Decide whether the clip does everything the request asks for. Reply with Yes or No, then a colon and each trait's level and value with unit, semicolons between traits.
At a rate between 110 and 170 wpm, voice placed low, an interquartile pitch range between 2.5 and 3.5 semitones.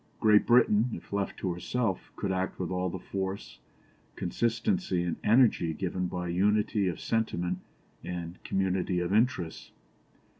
Yes: average, 140 wpm; very low, 95 Hz; average, 3.2 semitones